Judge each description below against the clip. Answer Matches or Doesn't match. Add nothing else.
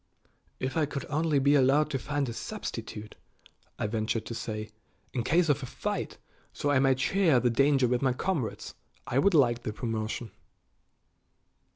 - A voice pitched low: Matches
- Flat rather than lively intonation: Doesn't match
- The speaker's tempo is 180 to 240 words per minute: Doesn't match